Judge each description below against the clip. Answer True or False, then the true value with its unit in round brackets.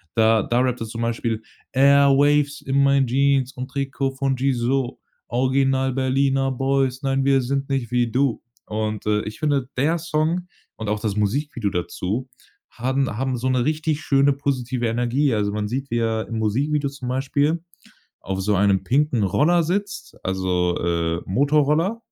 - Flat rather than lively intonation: False (3.5 semitones)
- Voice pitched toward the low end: True (130 Hz)